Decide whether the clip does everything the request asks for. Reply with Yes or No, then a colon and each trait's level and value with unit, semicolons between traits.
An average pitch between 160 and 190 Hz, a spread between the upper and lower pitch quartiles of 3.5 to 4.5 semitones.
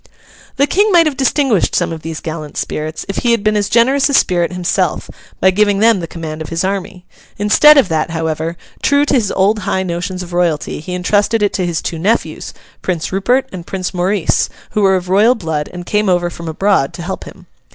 Yes: medium, 185 Hz; average, 4.0 semitones